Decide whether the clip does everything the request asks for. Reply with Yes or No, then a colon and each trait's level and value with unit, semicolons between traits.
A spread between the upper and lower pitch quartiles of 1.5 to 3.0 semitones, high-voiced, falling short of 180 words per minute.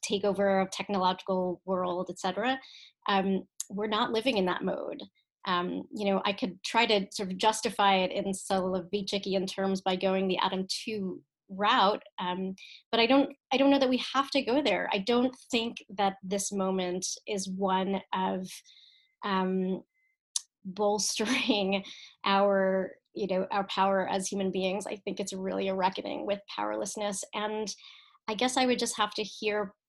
Yes: average, 2.7 semitones; high, 200 Hz; average, 165 wpm